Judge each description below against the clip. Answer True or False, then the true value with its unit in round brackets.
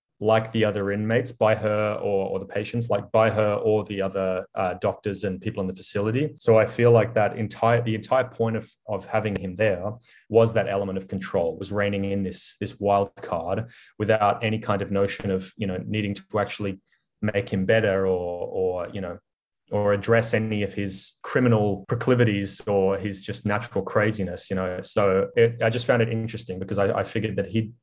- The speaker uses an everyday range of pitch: False (2.1 semitones)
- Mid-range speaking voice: False (105 Hz)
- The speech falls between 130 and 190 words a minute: False (205 wpm)